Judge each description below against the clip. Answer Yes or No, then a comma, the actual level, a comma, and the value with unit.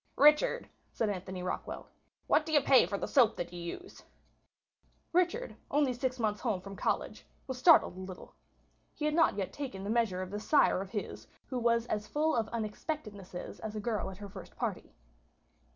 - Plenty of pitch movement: Yes, wide, 6.3 semitones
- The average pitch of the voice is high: Yes, high, 220 Hz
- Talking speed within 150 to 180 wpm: No, average, 190 wpm